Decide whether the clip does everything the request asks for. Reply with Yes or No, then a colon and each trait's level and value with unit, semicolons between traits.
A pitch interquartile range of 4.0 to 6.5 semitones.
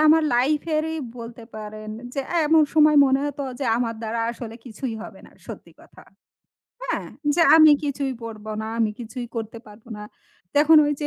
Yes: average, 5.0 semitones